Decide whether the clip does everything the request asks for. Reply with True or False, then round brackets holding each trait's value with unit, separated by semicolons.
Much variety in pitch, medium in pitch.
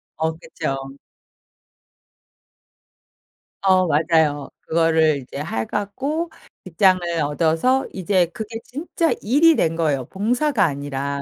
True (6.3 semitones; 170 Hz)